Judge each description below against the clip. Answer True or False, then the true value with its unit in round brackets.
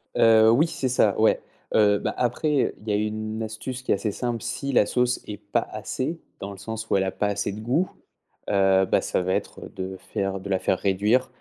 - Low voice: True (110 Hz)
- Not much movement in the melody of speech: False (3.7 semitones)